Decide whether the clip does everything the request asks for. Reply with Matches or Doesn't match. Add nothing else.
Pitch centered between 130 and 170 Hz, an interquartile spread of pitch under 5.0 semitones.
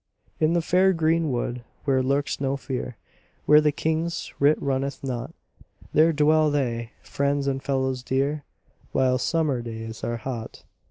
Matches